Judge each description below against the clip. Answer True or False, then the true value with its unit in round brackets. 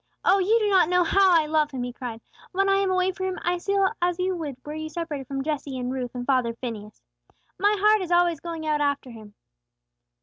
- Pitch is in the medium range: False (320 Hz)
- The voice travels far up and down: True (5.8 semitones)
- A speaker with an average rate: False (235 wpm)